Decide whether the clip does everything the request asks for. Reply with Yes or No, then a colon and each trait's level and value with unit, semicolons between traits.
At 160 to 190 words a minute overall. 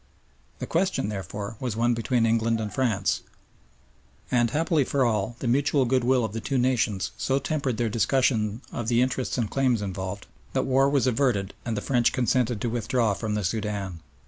Yes: average, 180 wpm